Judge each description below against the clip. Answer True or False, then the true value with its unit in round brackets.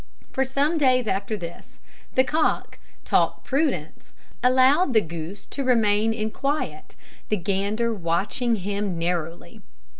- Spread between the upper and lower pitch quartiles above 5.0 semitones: True (5.4 semitones)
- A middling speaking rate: False (125 wpm)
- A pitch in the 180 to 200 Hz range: False (220 Hz)